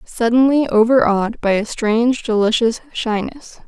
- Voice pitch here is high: Yes, high, 230 Hz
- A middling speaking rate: No, slow, 115 wpm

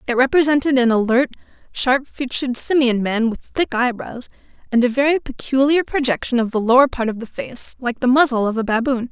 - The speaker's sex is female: Yes, female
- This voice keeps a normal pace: Yes, average, 190 wpm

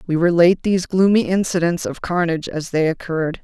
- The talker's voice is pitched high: No, medium, 170 Hz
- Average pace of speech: Yes, average, 175 wpm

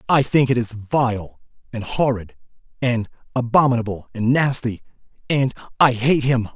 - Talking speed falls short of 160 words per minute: Yes, slow, 135 wpm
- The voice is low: Yes, low, 125 Hz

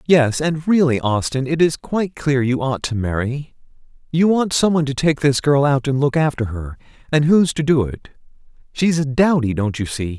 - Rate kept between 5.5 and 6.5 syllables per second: No, 5.0 syllables/s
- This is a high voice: No, medium, 140 Hz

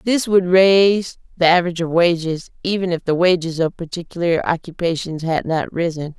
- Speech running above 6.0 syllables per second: No, 5.4 syllables/s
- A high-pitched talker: No, medium, 175 Hz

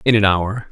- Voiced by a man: Yes, male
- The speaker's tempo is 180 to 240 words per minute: No, fast, 255 wpm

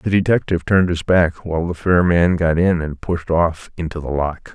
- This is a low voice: Yes, very low, 85 Hz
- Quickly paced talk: Yes, fast, 225 wpm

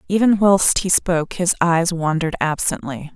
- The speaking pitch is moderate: Yes, medium, 175 Hz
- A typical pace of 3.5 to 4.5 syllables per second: No, 4.8 syllables/s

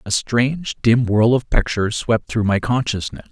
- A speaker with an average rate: Yes, average, 180 wpm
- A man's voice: Yes, male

